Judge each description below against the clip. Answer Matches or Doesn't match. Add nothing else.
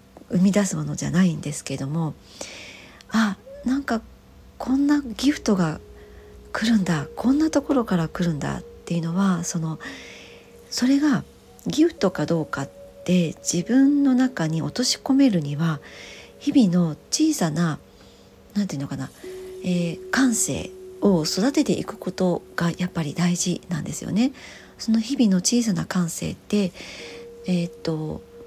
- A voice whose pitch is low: Doesn't match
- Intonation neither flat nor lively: Doesn't match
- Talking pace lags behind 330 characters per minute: Matches